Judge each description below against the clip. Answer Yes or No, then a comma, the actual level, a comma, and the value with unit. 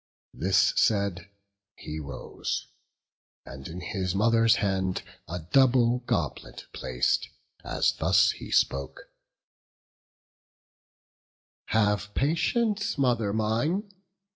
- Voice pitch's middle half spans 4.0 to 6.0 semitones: Yes, average, 5.1 semitones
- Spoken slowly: Yes, slow, 90 wpm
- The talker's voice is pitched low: Yes, low, 105 Hz